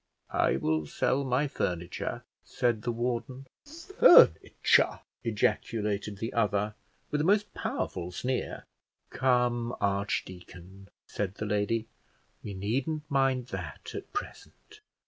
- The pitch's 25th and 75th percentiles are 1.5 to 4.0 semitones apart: No, average, 4.7 semitones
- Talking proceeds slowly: Yes, slow, 110 wpm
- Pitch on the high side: No, low, 115 Hz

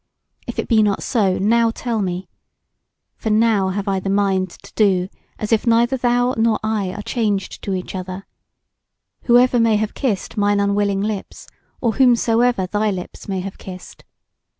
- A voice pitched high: Yes, high, 210 Hz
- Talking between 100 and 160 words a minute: No, average, 170 wpm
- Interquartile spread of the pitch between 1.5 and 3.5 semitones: Yes, average, 2.9 semitones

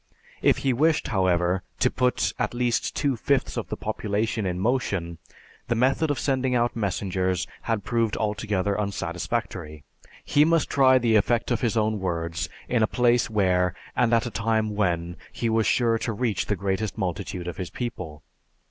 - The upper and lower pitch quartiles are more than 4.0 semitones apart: Yes, average, 4.6 semitones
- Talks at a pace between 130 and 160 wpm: No, average, 175 wpm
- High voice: No, low, 110 Hz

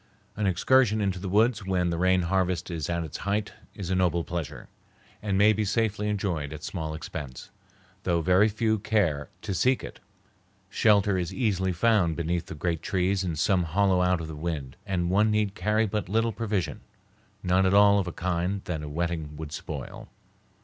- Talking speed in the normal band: Yes, average, 190 wpm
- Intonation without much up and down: No, average, 3.4 semitones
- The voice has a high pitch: No, very low, 95 Hz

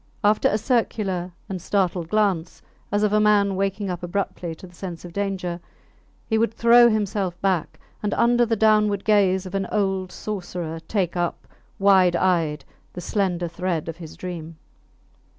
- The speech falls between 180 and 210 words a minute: No, average, 165 wpm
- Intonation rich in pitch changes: No, average, 3.0 semitones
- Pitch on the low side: No, high, 190 Hz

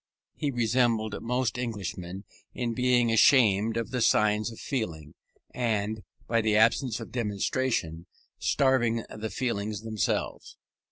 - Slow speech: Yes, slow, 120 wpm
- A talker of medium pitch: No, low, 115 Hz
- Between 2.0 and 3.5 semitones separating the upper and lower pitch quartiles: Yes, average, 2.7 semitones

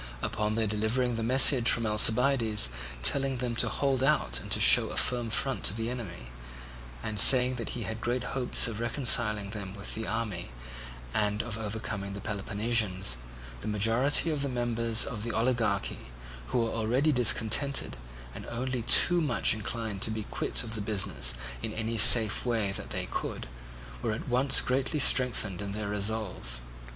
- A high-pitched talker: No, low, 115 Hz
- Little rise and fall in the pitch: No, average, 3.0 semitones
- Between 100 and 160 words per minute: No, average, 170 wpm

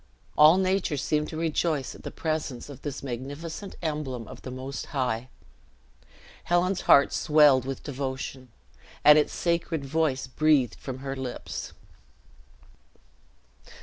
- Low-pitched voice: No, medium, 145 Hz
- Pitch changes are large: No, average, 3.2 semitones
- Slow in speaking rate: Yes, slow, 125 wpm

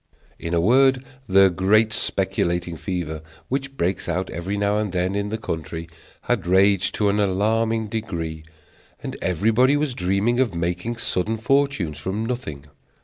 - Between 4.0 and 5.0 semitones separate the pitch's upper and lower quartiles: Yes, average, 4.3 semitones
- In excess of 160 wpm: No, average, 150 wpm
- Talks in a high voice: No, low, 100 Hz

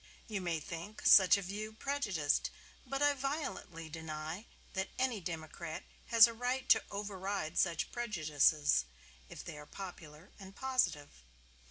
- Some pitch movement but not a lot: No, wide, 6.3 semitones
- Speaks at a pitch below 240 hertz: Yes, high, 190 Hz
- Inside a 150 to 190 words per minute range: No, average, 140 wpm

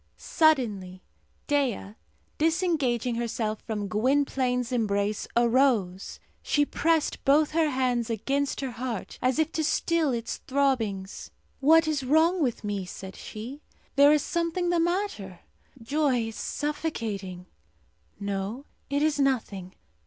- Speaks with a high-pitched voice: Yes, very high, 255 Hz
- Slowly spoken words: Yes, slow, 125 wpm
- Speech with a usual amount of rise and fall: No, wide, 5.8 semitones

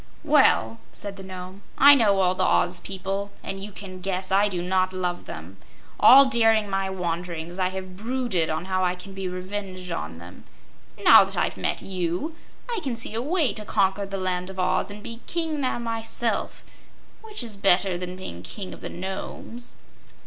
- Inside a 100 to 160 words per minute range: No, average, 190 wpm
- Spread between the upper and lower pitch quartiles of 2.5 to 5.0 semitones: Yes, average, 3.1 semitones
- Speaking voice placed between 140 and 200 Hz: Yes, high, 190 Hz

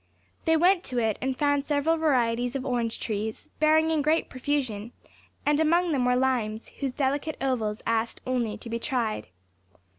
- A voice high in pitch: Yes, very high, 260 Hz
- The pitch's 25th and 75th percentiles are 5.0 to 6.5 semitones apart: No, average, 4.3 semitones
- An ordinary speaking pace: Yes, average, 170 wpm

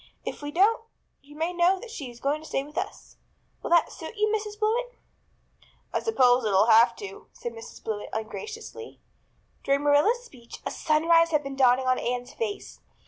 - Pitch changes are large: Yes, wide, 9.0 semitones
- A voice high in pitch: Yes, very high, 300 Hz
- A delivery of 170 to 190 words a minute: Yes, average, 185 wpm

